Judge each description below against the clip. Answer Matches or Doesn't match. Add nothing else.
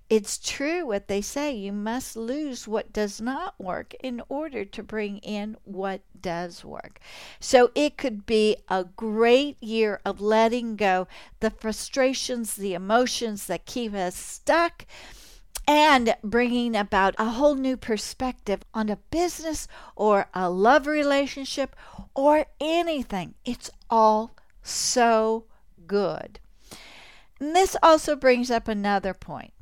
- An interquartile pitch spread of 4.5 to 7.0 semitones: Matches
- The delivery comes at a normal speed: Doesn't match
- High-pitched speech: Matches